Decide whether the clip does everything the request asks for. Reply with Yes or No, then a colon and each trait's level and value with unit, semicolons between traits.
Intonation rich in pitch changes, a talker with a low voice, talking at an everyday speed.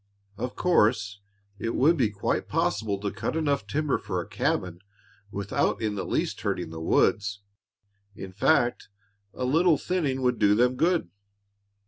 Yes: wide, 6.2 semitones; low, 115 Hz; average, 150 wpm